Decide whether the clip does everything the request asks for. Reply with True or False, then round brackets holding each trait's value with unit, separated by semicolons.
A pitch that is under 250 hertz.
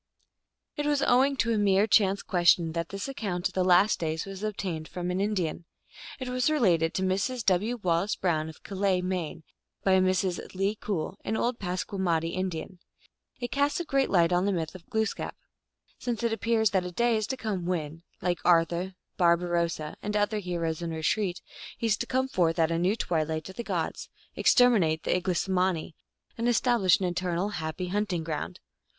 True (185 Hz)